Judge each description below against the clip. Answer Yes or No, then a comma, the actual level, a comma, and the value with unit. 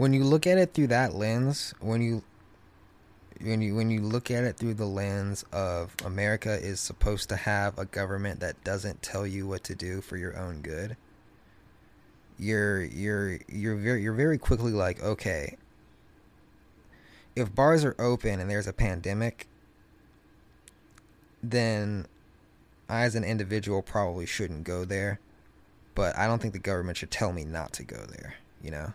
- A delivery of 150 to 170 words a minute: Yes, average, 165 wpm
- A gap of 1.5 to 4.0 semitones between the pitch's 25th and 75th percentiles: Yes, average, 2.9 semitones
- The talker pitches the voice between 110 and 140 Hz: No, low, 100 Hz